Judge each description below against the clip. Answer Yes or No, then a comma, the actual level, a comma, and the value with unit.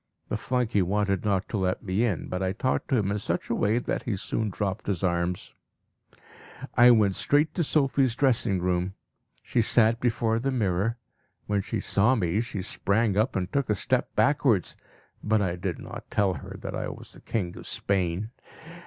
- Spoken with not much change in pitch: No, average, 3.9 semitones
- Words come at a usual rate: Yes, average, 190 wpm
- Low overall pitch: Yes, low, 105 Hz